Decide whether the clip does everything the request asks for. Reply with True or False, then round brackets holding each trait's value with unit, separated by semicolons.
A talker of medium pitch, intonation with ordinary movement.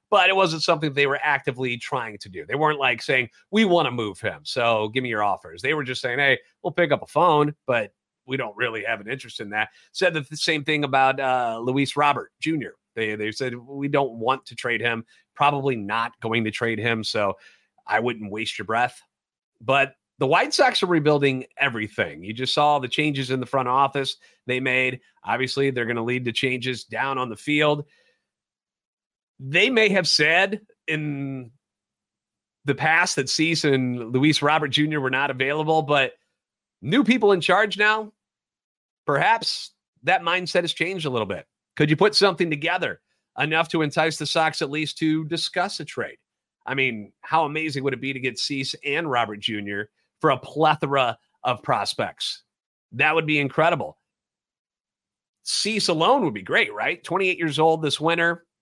True (145 Hz; 4.1 semitones)